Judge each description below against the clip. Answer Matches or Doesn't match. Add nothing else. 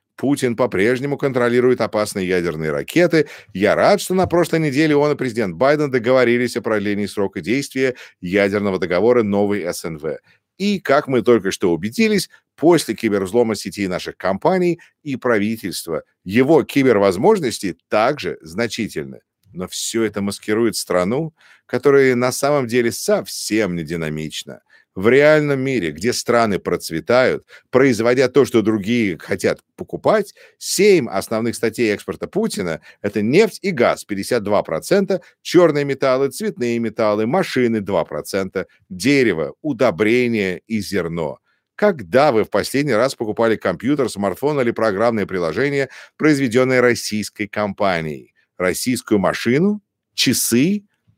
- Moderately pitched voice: Doesn't match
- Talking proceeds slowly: Matches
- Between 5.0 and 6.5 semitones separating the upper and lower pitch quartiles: Matches